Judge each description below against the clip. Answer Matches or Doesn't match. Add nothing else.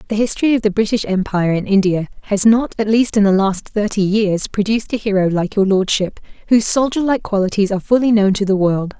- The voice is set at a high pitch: Matches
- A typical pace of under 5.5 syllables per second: Doesn't match